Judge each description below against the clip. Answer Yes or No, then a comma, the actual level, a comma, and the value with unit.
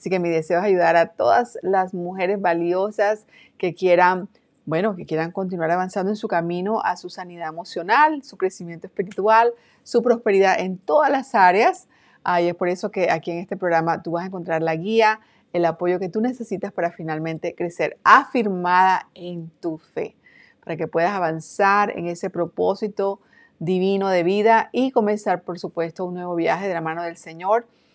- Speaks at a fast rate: No, average, 180 wpm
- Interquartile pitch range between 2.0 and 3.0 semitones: No, average, 3.4 semitones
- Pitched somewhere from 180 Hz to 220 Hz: Yes, medium, 185 Hz